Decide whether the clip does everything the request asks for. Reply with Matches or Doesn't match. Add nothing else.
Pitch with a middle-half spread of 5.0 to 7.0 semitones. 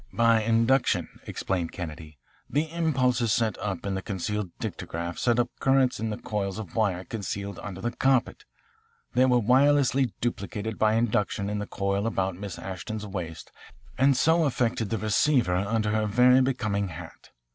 Doesn't match